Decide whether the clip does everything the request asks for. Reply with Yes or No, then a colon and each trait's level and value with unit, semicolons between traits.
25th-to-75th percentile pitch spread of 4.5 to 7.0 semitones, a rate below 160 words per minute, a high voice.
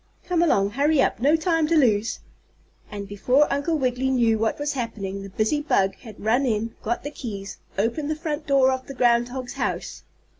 No: average, 5.1 semitones; average, 190 wpm; very high, 250 Hz